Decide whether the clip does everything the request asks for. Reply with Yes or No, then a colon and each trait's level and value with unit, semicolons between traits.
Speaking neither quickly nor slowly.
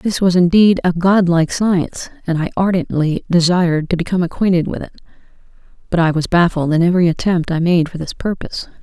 Yes: average, 185 wpm